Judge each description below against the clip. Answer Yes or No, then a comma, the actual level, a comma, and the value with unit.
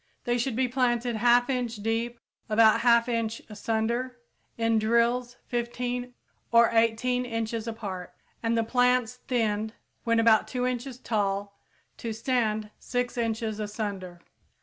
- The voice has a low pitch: No, high, 230 Hz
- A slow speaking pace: Yes, slow, 130 wpm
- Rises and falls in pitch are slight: Yes, narrow, 1.9 semitones